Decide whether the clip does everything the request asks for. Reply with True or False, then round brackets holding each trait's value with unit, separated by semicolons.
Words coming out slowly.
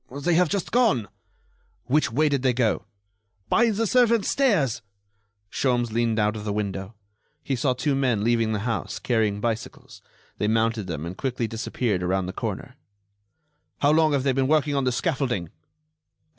False (170 wpm)